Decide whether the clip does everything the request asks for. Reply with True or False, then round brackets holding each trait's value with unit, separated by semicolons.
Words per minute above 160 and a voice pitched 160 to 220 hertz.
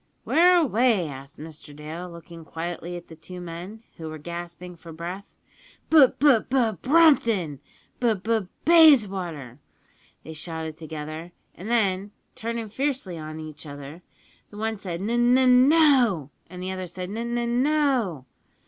False (155 wpm; 185 Hz)